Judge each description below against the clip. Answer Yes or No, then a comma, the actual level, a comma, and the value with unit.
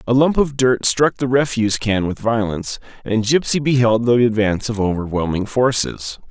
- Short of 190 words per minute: Yes, average, 170 wpm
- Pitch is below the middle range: Yes, low, 115 Hz